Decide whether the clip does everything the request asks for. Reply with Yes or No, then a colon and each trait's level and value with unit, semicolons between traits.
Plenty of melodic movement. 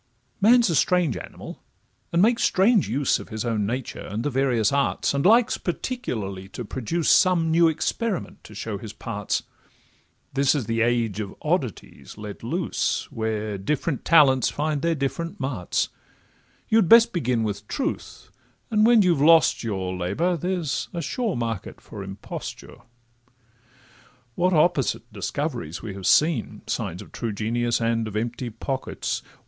Yes: wide, 7.5 semitones